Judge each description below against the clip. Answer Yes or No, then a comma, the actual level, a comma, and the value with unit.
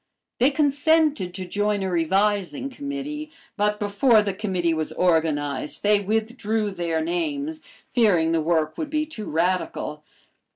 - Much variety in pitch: Yes, wide, 5.9 semitones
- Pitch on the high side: Yes, high, 200 Hz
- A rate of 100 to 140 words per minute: Yes, slow, 135 wpm